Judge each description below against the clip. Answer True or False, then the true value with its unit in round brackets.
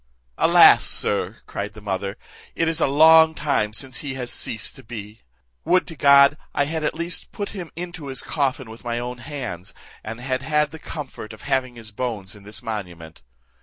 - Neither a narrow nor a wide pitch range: False (5.7 semitones)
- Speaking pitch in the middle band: False (130 Hz)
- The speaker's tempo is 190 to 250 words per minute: True (195 wpm)